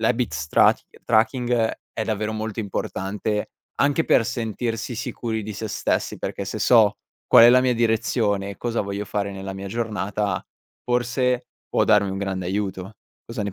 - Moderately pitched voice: No, low, 110 Hz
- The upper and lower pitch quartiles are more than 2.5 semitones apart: Yes, average, 2.9 semitones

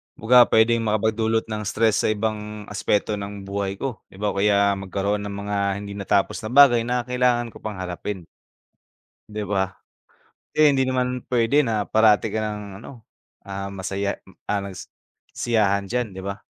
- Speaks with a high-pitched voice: No, low, 105 Hz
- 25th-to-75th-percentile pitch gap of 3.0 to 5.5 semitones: No, narrow, 2.6 semitones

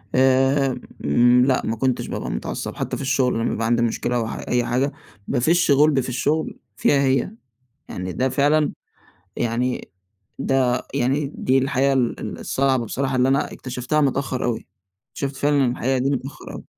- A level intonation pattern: Yes, narrow, 2.0 semitones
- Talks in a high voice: No, low, 130 Hz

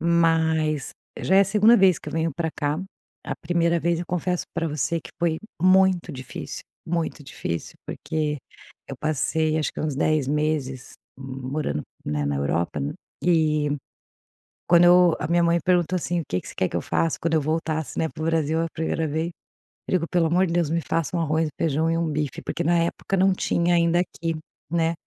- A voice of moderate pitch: Yes, medium, 160 Hz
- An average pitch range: No, narrow, 2.2 semitones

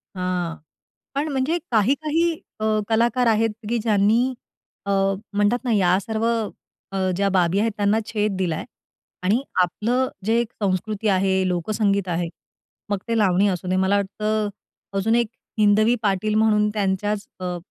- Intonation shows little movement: No, average, 3.0 semitones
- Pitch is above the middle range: Yes, high, 210 Hz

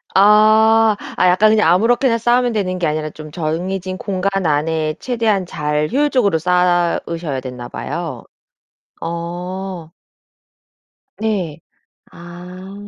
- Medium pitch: Yes, medium, 180 Hz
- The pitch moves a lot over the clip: No, average, 4.4 semitones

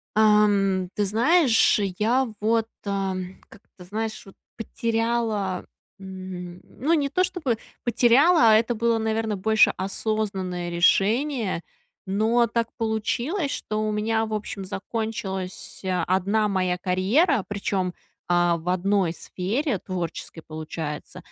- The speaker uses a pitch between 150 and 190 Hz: No, high, 210 Hz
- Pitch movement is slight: No, average, 3.6 semitones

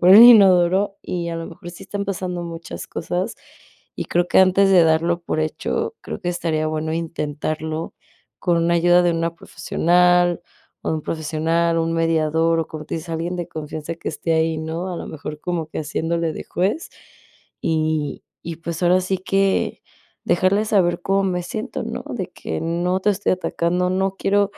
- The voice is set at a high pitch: No, medium, 170 Hz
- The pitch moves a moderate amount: No, narrow, 2.2 semitones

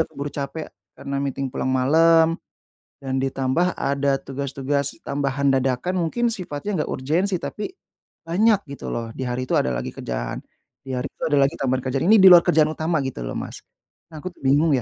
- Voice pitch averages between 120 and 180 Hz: Yes, medium, 140 Hz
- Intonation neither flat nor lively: Yes, average, 3.8 semitones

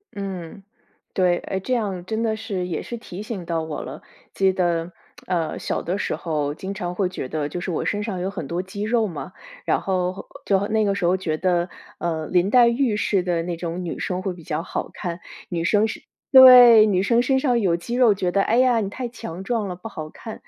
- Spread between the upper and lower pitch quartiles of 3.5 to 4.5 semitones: Yes, average, 3.8 semitones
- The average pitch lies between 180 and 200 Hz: Yes, high, 190 Hz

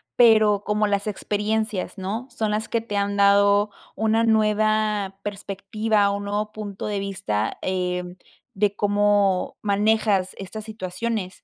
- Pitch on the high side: Yes, high, 205 Hz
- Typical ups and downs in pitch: No, narrow, 1.5 semitones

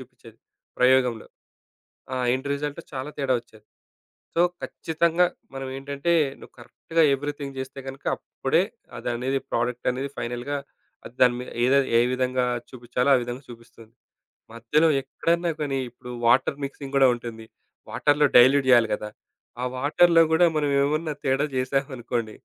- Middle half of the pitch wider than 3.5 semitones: No, average, 2.9 semitones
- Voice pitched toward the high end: No, low, 135 Hz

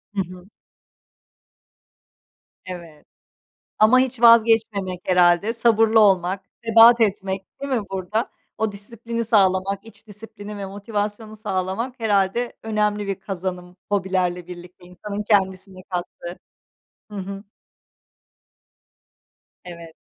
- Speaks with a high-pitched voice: Yes, high, 200 Hz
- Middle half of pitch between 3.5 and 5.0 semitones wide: No, average, 3.1 semitones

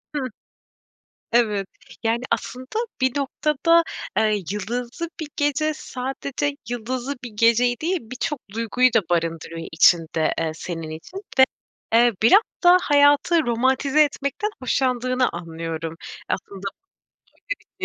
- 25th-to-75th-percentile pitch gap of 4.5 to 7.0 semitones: Yes, wide, 5.6 semitones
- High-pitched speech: Yes, high, 245 Hz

